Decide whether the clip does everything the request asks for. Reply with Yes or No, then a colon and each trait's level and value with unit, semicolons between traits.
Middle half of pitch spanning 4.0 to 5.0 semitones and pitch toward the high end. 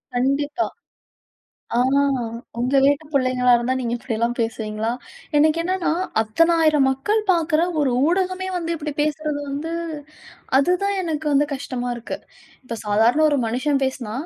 Yes: average, 4.5 semitones; very high, 280 Hz